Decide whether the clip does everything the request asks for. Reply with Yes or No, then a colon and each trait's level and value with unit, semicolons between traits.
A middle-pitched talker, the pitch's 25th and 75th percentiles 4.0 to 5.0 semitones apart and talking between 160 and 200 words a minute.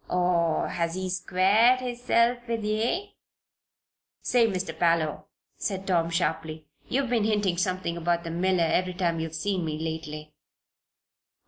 No: medium, 180 Hz; average, 4.3 semitones; slow, 135 wpm